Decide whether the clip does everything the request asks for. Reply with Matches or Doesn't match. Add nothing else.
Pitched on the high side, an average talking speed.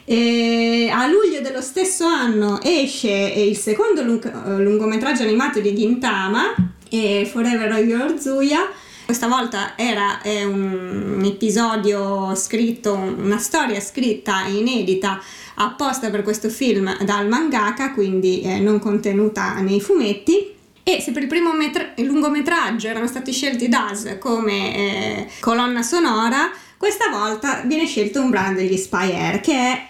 Matches